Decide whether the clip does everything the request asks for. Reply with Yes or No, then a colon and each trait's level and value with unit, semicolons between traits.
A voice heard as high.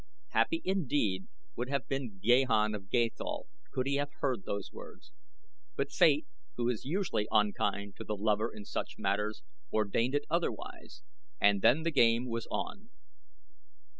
No: low, 120 Hz